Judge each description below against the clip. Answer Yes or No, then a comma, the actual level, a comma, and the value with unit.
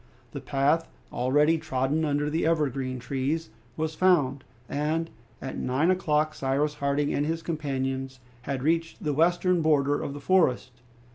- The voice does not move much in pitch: No, average, 3.2 semitones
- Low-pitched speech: No, medium, 150 Hz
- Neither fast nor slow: Yes, average, 145 wpm